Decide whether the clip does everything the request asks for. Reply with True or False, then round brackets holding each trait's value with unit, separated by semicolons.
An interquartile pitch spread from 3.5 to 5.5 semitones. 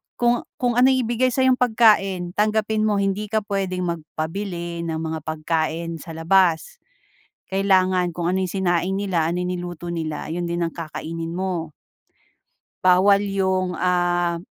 False (3.0 semitones)